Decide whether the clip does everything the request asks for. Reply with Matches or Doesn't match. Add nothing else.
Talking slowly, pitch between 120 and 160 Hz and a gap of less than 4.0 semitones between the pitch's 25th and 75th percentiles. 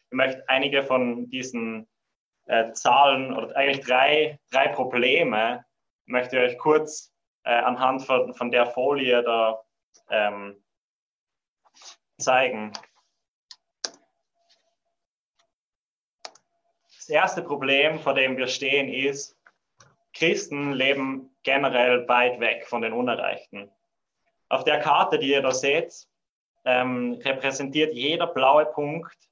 Matches